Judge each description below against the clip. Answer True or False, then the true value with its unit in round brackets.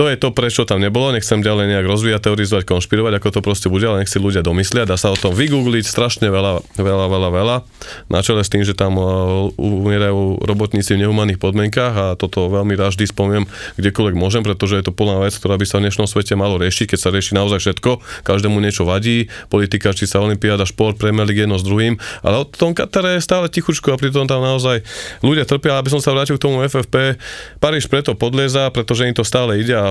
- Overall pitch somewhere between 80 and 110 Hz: True (105 Hz)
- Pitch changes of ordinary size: True (3.5 semitones)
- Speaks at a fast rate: True (220 wpm)